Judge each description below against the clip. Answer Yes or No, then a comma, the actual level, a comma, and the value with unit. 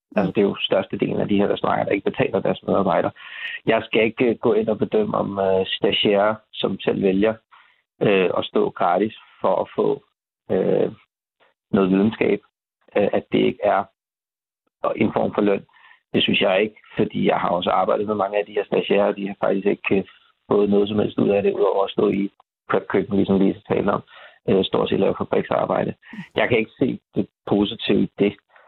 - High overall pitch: No, low, 100 Hz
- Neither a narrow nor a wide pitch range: No, narrow, 1.4 semitones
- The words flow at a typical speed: Yes, average, 210 wpm